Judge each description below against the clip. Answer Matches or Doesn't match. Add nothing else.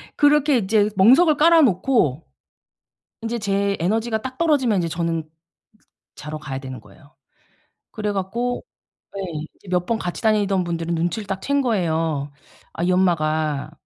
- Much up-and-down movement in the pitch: Matches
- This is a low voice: Doesn't match